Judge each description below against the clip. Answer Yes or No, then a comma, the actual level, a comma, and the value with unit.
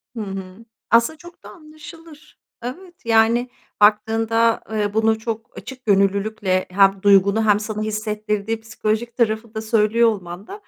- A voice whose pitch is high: Yes, high, 220 Hz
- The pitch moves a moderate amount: No, narrow, 2.1 semitones